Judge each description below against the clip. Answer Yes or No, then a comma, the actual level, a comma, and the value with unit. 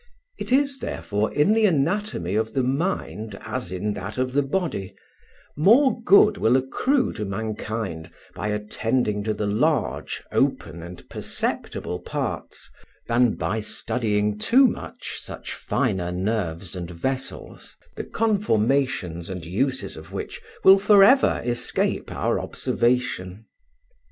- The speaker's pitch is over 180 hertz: No, low, 110 Hz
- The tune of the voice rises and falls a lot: Yes, wide, 8.0 semitones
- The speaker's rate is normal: No, slow, 130 wpm